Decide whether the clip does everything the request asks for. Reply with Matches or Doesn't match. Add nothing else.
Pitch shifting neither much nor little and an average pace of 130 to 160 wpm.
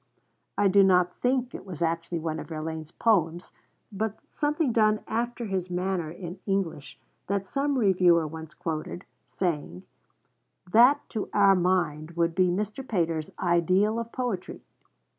Matches